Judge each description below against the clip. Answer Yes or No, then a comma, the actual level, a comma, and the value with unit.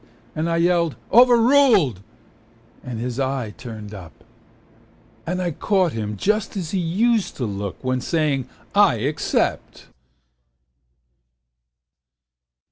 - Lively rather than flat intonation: Yes, wide, 8.2 semitones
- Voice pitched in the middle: Yes, medium, 155 Hz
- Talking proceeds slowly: Yes, slow, 110 wpm